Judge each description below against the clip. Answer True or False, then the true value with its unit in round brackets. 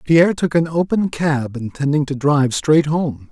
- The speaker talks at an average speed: True (180 wpm)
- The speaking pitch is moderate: True (150 Hz)